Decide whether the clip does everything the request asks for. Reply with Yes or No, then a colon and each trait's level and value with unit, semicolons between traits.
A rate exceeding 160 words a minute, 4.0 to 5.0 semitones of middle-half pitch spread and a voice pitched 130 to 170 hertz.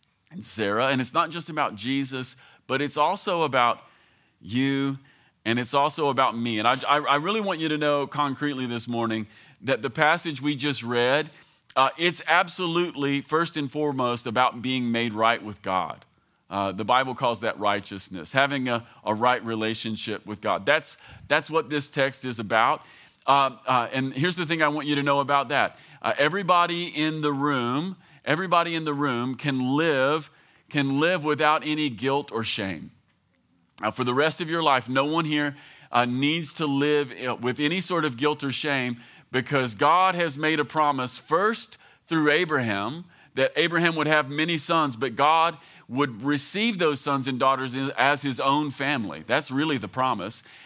No: average, 180 wpm; average, 3.6 semitones; medium, 140 Hz